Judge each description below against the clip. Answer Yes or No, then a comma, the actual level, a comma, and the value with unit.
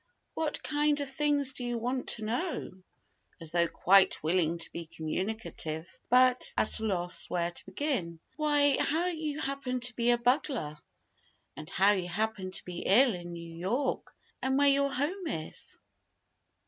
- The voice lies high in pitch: Yes, high, 235 Hz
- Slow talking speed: No, average, 165 wpm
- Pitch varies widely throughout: Yes, wide, 8.1 semitones